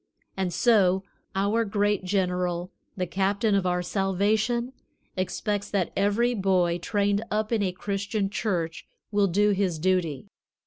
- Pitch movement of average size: No, narrow, 2.3 semitones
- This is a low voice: No, high, 195 Hz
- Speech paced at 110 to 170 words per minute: Yes, slow, 135 wpm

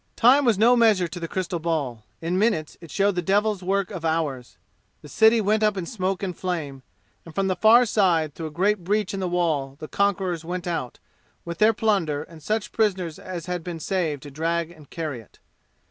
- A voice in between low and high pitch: Yes, medium, 180 Hz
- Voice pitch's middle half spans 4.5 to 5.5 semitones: No, average, 4.0 semitones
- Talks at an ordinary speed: No, fast, 210 wpm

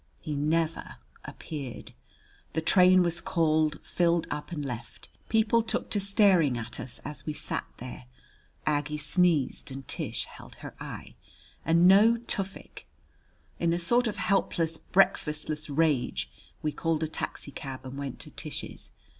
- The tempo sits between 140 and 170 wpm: Yes, average, 145 wpm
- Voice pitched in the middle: Yes, medium, 160 Hz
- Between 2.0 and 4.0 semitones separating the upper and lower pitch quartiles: Yes, average, 3.7 semitones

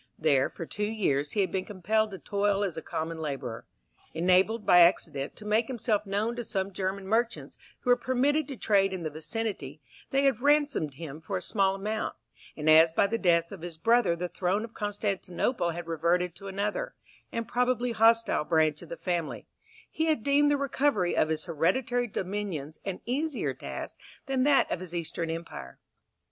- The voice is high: Yes, high, 195 Hz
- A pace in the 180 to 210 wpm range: Yes, average, 185 wpm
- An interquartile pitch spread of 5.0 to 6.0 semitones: Yes, wide, 5.5 semitones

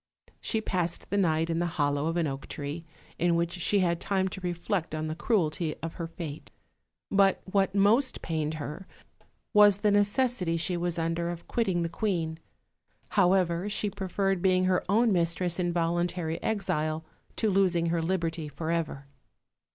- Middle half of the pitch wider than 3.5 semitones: No, average, 2.9 semitones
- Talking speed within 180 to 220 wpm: No, average, 165 wpm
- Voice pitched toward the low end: No, medium, 175 Hz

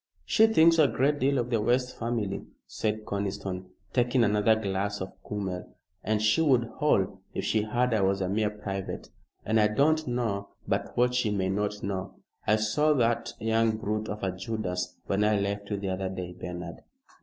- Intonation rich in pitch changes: No, average, 3.5 semitones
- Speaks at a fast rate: No, average, 190 wpm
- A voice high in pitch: No, low, 105 Hz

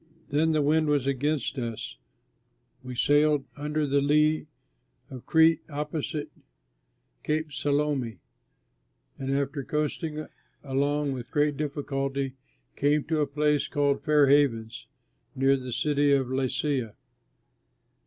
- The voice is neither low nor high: Yes, medium, 145 Hz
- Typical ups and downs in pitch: No, narrow, 1.8 semitones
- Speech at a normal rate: No, slow, 120 wpm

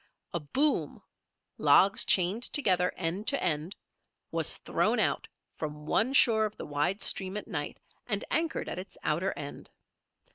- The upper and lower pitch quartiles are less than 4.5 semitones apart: No, average, 5.1 semitones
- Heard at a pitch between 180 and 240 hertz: Yes, high, 190 Hz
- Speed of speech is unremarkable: Yes, average, 150 wpm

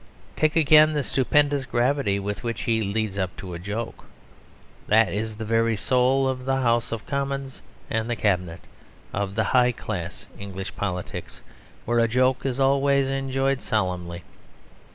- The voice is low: Yes, low, 115 Hz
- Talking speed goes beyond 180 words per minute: No, average, 155 wpm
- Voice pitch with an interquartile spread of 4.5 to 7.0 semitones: Yes, average, 4.9 semitones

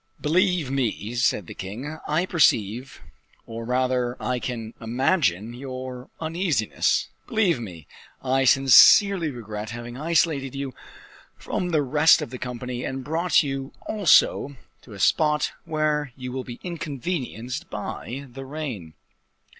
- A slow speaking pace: Yes, slow, 130 wpm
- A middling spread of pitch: Yes, average, 4.2 semitones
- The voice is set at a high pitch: No, low, 130 Hz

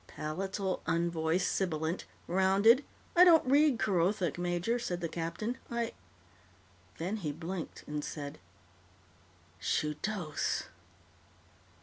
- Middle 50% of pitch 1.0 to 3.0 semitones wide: No, average, 5.0 semitones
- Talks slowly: Yes, slow, 105 wpm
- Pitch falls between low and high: Yes, medium, 175 Hz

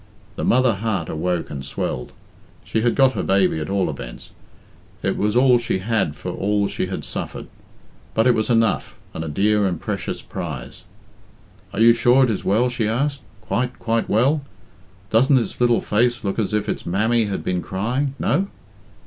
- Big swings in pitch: No, average, 4.1 semitones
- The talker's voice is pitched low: Yes, low, 110 Hz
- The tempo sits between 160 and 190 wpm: Yes, average, 185 wpm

